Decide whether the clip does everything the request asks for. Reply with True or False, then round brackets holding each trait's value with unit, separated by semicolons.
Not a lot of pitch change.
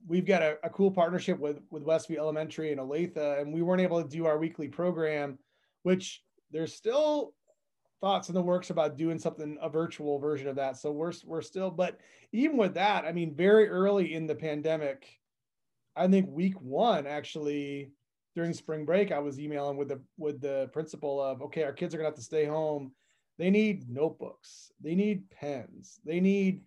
False (3.8 semitones)